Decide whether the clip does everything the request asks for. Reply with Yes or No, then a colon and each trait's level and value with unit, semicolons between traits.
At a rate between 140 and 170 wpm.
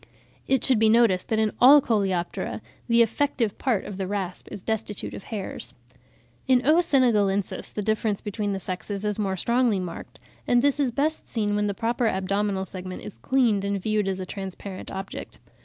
No: average, 185 wpm